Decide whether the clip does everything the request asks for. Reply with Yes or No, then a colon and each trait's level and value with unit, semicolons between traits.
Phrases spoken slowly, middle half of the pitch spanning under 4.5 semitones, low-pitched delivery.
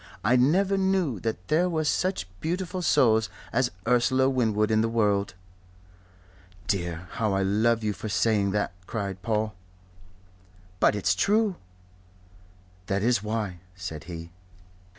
No: slow, 130 wpm; average, 5.0 semitones; low, 110 Hz